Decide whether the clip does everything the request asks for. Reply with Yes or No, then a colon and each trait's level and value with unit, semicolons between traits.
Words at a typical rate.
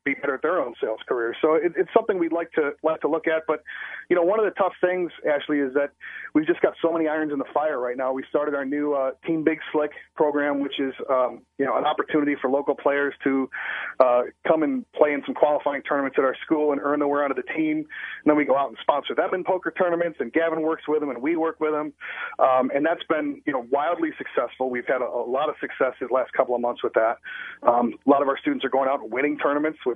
No: fast, 270 wpm